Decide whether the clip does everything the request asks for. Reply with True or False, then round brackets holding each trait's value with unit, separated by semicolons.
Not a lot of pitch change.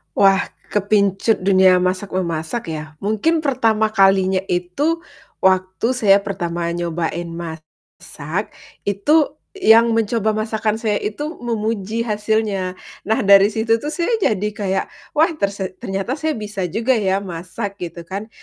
False (3.1 semitones)